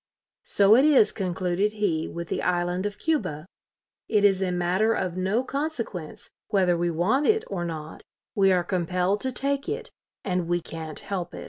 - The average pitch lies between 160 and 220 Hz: Yes, medium, 185 Hz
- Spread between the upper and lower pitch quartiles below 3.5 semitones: No, average, 3.8 semitones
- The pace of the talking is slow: No, average, 180 wpm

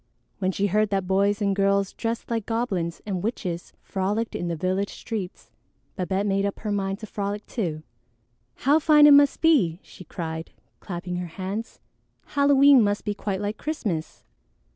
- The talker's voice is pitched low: No, high, 200 Hz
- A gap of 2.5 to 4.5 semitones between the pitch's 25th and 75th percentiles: Yes, average, 3.4 semitones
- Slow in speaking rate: No, average, 165 wpm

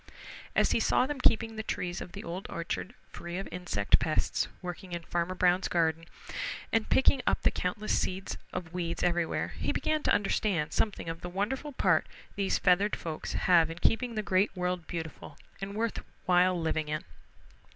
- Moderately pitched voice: Yes, medium, 180 Hz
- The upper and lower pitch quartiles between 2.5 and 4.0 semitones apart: Yes, average, 3.5 semitones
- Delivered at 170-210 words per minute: Yes, average, 180 wpm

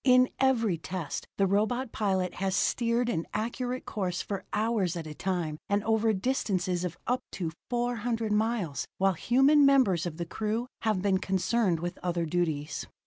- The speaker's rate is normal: Yes, average, 160 wpm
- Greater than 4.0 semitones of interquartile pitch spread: Yes, average, 4.9 semitones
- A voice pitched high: Yes, high, 205 Hz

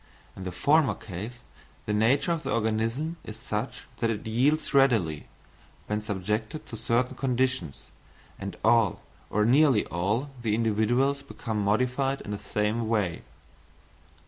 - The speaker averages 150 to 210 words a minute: No, average, 140 wpm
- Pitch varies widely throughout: No, average, 3.8 semitones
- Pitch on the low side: Yes, low, 115 Hz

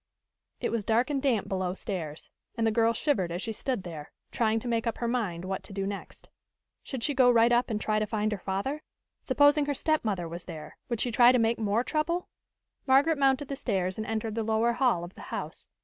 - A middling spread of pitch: Yes, average, 4.5 semitones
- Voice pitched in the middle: No, high, 225 Hz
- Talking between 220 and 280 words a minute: Yes, fast, 225 wpm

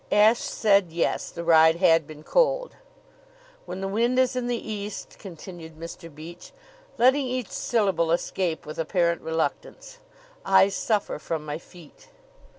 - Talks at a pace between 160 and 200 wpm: No, average, 145 wpm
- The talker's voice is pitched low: No, medium, 185 Hz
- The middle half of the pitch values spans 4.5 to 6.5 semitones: Yes, average, 5.2 semitones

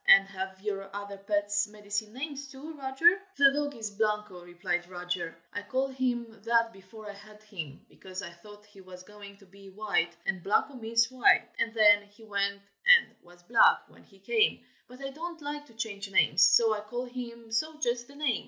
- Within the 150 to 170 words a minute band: No, average, 200 wpm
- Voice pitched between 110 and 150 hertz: No, high, 210 Hz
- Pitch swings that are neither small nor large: Yes, average, 3.9 semitones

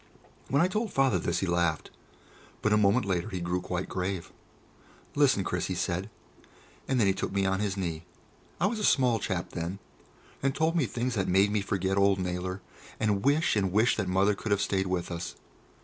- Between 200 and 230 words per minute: Yes, fast, 205 wpm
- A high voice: No, very low, 95 Hz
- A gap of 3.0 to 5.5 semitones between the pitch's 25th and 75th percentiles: Yes, average, 3.7 semitones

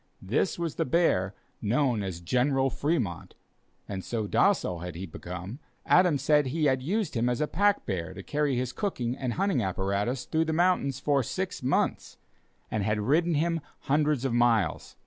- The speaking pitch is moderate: No, low, 130 Hz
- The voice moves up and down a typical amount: No, wide, 6.9 semitones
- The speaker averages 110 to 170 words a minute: No, average, 180 wpm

